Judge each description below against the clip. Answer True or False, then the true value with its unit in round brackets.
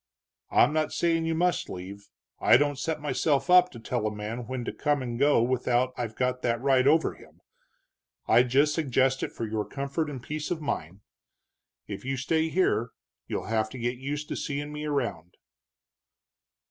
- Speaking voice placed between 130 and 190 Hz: True (135 Hz)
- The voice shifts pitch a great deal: False (4.0 semitones)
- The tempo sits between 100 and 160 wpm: False (185 wpm)